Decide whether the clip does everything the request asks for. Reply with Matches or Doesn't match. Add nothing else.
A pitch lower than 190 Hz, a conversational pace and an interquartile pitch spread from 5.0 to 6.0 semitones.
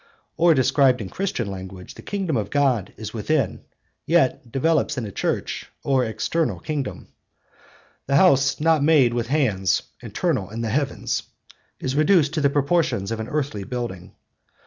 Matches